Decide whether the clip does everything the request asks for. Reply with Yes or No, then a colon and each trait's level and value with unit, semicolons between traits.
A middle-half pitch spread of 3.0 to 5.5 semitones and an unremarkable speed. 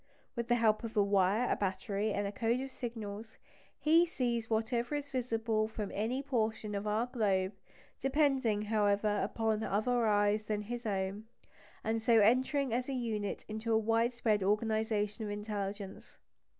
No: narrow, 2.5 semitones; average, 160 wpm